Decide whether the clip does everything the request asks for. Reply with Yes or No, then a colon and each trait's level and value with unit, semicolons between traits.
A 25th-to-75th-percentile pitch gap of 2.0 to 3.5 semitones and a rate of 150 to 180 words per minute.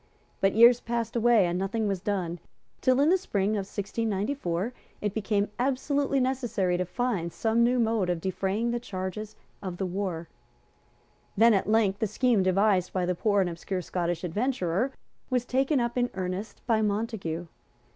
No: average, 4.2 semitones; average, 165 wpm